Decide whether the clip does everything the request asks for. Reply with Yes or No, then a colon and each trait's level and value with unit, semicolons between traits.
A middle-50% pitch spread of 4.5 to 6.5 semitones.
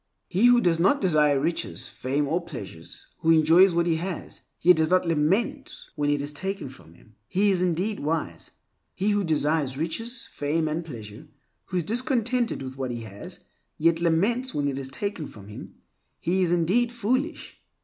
Yes: average, 5.1 semitones